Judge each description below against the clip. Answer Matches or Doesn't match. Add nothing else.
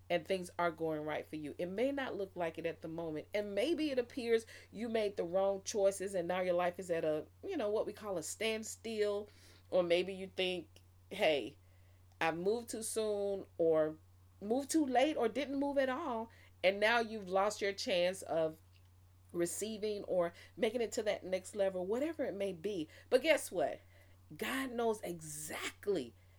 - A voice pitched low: Doesn't match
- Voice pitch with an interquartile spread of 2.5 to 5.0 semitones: Doesn't match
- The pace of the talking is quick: Doesn't match